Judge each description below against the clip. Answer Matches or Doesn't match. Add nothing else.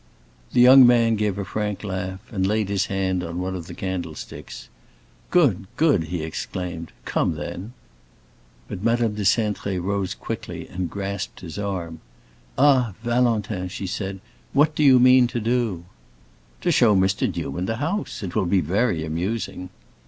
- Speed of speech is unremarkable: Matches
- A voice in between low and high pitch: Doesn't match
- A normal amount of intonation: Matches